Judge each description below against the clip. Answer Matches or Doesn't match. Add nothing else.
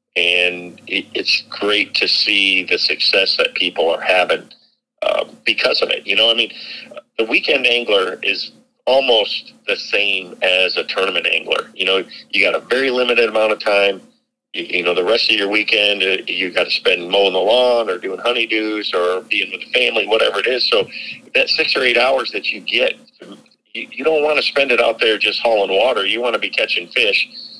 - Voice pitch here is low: Doesn't match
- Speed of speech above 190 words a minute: Matches